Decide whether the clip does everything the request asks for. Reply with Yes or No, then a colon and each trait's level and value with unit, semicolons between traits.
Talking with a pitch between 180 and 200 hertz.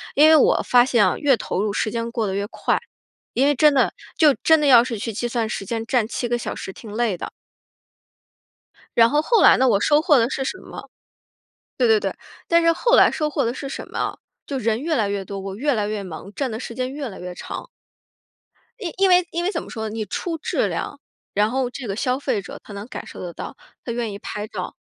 No: high, 240 Hz